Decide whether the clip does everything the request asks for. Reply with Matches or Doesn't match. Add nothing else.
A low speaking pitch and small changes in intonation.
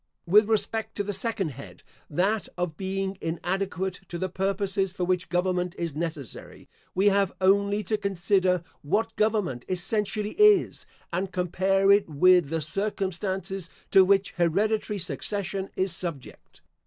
Doesn't match